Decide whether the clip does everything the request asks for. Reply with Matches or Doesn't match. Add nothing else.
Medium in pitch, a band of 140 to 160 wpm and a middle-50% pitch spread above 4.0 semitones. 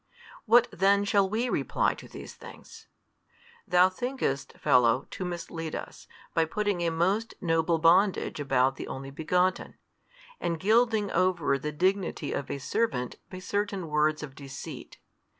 Matches